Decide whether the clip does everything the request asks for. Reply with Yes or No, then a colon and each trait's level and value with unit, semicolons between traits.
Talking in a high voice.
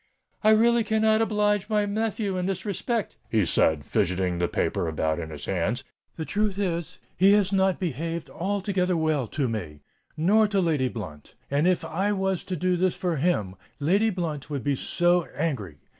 No: medium, 175 Hz